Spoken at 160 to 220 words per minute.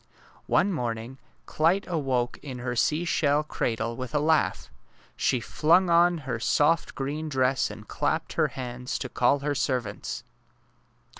No: average, 140 wpm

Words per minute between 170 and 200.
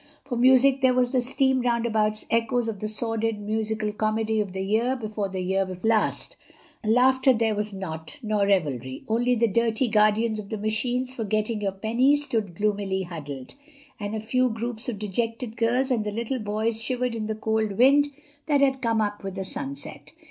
Yes: average, 175 wpm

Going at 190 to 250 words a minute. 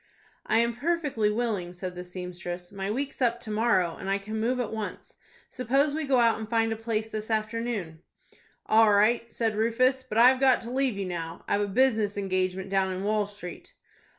Yes: average, 200 wpm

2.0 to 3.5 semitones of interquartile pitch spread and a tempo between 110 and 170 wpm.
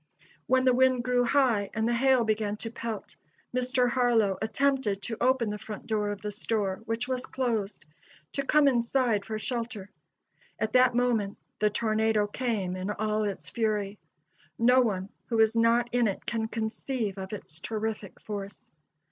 Yes: average, 2.9 semitones; average, 165 wpm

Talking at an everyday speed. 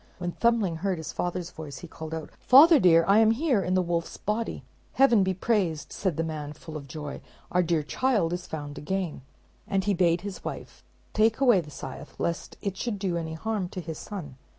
No: fast, 210 wpm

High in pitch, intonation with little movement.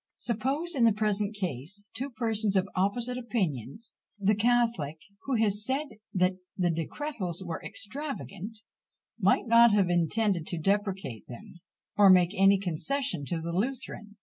No: high, 205 Hz; average, 4.5 semitones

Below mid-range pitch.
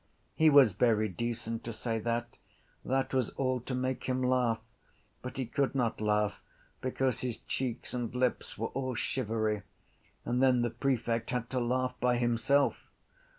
Yes: low, 125 Hz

